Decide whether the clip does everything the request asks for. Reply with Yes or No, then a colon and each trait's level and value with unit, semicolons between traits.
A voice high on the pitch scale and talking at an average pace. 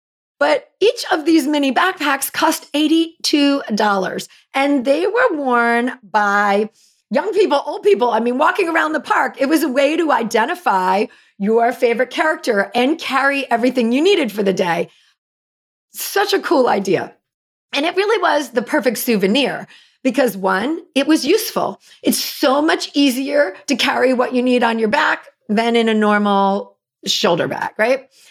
Yes: very high, 270 Hz; average, 160 wpm